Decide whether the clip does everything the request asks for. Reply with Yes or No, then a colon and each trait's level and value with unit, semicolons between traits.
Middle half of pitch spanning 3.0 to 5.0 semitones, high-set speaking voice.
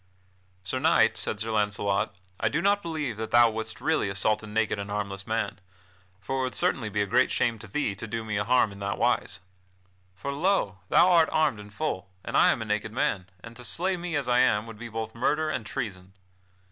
No: average, 4.3 semitones; low, 110 Hz